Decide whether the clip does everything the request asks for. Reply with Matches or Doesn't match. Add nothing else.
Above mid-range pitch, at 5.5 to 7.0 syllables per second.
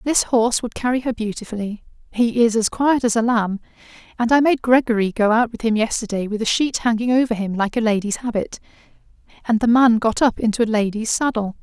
Matches